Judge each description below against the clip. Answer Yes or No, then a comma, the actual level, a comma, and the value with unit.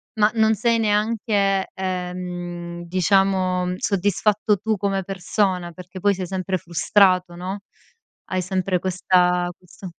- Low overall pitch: No, medium, 185 Hz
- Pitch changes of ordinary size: No, narrow, 1.9 semitones